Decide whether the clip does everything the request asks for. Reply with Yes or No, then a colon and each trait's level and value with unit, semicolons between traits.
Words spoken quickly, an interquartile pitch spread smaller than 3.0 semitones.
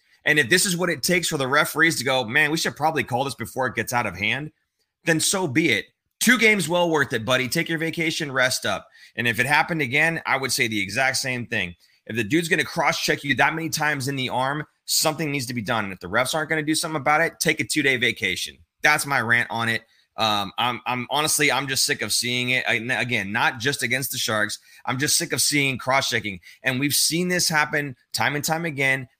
No: fast, 255 wpm; average, 4.4 semitones